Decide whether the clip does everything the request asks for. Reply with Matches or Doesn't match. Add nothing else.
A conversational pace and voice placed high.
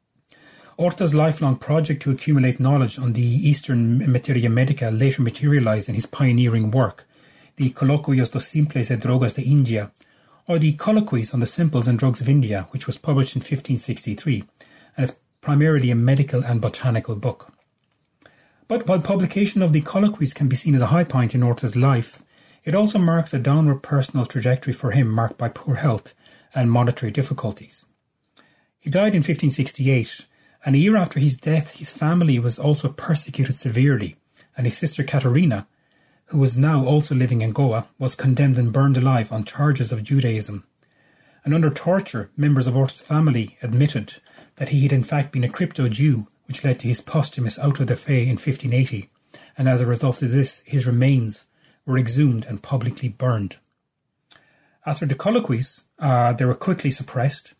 Doesn't match